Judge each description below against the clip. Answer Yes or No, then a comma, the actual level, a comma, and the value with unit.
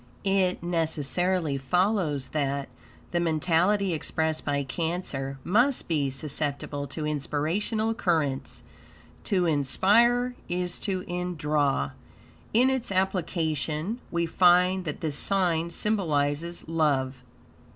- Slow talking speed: Yes, slow, 100 wpm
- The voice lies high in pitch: No, medium, 165 Hz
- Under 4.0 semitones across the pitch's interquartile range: No, average, 4.3 semitones